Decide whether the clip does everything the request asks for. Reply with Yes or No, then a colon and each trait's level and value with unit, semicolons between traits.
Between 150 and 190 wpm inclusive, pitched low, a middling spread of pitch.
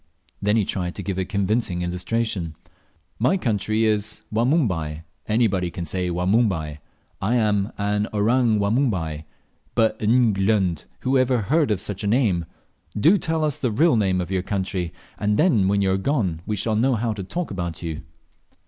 Yes: average, 170 wpm; low, 105 Hz; average, 4.1 semitones